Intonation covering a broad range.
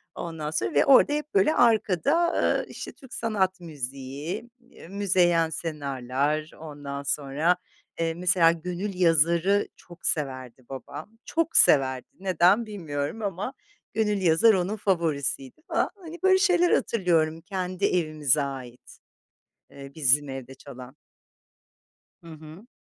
Yes: wide, 6.0 semitones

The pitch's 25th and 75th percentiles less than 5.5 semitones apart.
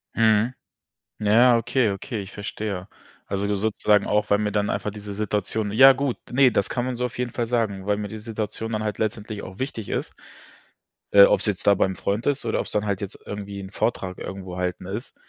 Yes: narrow, 2.4 semitones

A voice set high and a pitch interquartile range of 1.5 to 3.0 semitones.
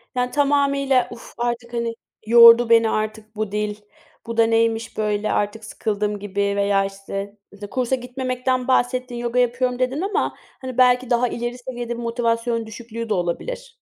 Yes: high, 235 Hz; narrow, 2.6 semitones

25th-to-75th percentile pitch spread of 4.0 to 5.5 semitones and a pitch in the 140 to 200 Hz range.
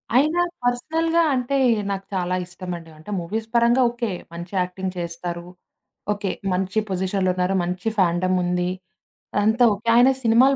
Yes: average, 4.9 semitones; high, 190 Hz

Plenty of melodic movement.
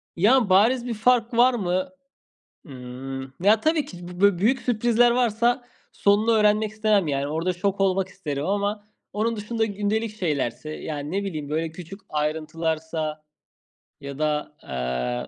Yes: wide, 6.1 semitones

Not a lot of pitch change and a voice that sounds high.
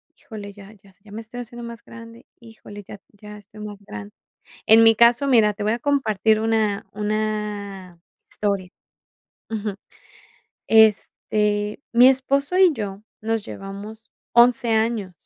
Yes: narrow, 2.1 semitones; high, 215 Hz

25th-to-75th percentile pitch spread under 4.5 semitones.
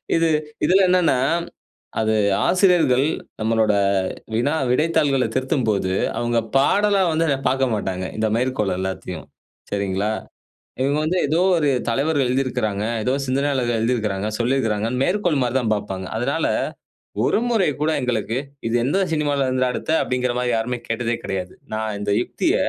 No: average, 4.8 semitones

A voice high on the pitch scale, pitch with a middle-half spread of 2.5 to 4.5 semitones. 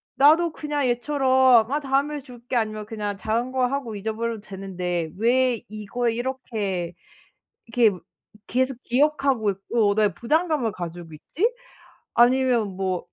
Yes: high, 235 Hz; average, 4.1 semitones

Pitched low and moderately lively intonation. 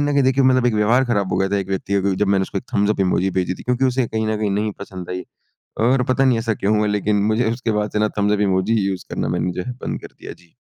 Yes: low, 105 Hz; average, 3.7 semitones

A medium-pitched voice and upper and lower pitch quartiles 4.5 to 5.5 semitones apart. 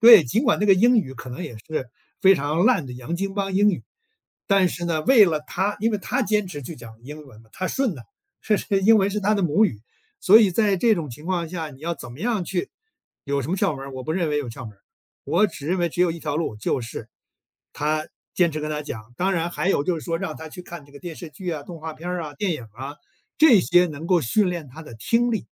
Yes: medium, 170 Hz; average, 5.1 semitones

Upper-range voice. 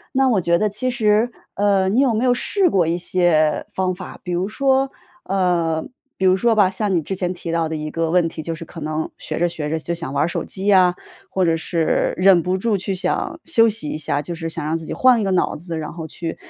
No: medium, 180 Hz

